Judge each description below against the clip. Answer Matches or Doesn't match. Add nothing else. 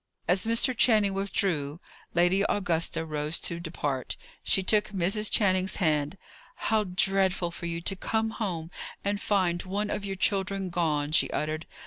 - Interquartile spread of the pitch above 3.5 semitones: Doesn't match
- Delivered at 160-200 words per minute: Doesn't match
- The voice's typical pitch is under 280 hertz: Matches